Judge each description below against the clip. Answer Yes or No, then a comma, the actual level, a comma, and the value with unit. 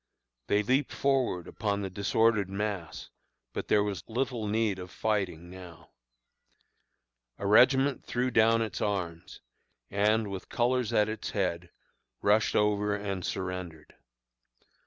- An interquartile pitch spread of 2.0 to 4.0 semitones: Yes, average, 3.2 semitones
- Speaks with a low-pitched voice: Yes, low, 105 Hz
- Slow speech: Yes, slow, 125 wpm